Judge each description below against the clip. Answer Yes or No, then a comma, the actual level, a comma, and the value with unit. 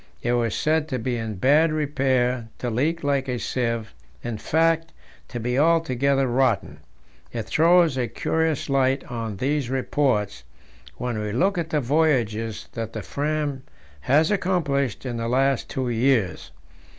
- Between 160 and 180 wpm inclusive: No, average, 150 wpm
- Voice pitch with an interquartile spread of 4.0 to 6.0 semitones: Yes, average, 4.4 semitones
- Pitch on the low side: Yes, low, 130 Hz